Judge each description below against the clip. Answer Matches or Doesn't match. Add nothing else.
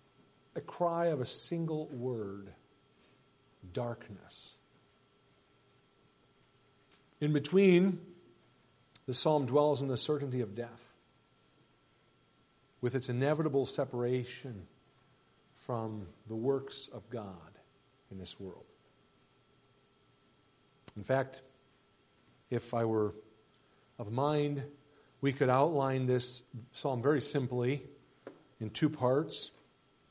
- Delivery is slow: Matches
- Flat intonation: Matches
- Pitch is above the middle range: Doesn't match